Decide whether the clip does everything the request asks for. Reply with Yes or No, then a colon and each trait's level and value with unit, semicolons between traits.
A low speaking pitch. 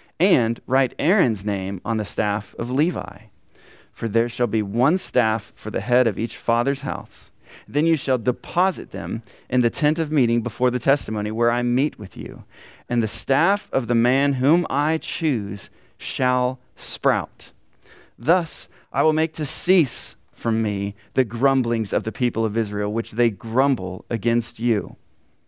Yes: low, 120 Hz